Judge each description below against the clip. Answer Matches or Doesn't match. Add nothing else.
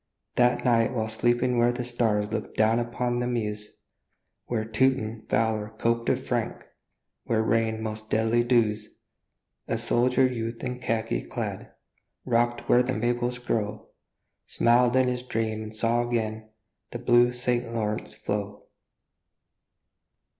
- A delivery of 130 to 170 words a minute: Matches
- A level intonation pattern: Matches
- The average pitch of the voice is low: Matches